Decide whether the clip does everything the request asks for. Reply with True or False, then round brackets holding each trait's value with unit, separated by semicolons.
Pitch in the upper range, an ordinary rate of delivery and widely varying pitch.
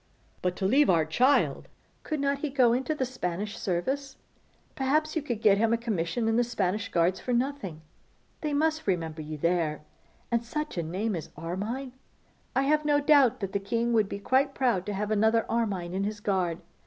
True (225 Hz; 190 wpm; 6.5 semitones)